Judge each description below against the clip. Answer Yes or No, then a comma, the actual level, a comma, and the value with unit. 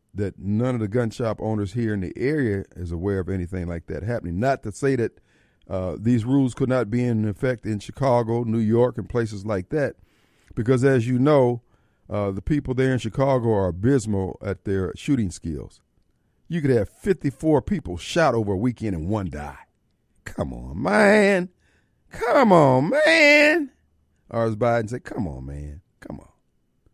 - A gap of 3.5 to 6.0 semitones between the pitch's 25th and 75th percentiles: Yes, average, 5.3 semitones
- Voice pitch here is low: Yes, low, 115 Hz